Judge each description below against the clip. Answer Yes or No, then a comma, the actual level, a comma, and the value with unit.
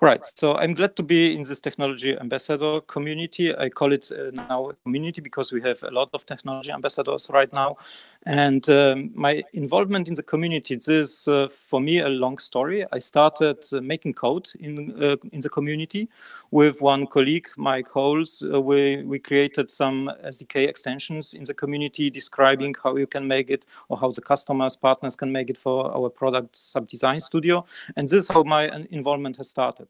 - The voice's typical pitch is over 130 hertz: Yes, medium, 140 Hz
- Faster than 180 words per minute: Yes, average, 190 wpm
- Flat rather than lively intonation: Yes, narrow, 2.2 semitones